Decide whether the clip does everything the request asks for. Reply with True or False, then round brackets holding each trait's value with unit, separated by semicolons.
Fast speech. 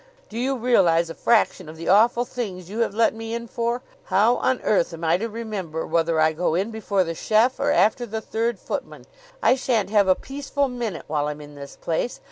True (220 wpm)